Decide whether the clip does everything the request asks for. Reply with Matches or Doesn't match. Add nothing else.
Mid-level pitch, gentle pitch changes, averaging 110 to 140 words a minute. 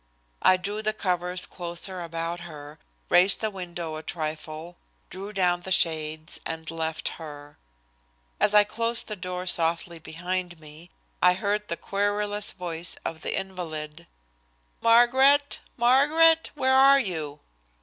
Doesn't match